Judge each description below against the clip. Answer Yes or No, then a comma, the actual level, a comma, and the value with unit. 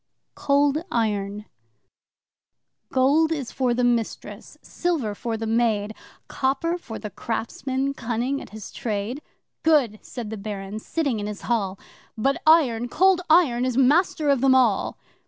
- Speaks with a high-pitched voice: Yes, high, 245 Hz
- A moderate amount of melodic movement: Yes, average, 4.3 semitones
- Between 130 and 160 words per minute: Yes, average, 140 wpm